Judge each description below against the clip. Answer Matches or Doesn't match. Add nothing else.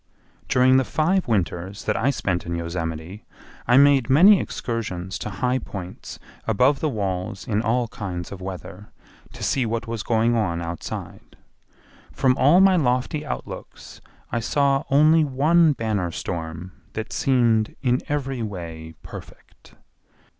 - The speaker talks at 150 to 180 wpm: Doesn't match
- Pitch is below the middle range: Matches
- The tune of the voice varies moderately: Doesn't match